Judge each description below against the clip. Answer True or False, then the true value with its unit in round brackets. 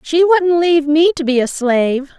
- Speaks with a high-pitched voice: True (305 Hz)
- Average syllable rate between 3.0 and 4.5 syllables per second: False (5.1 syllables/s)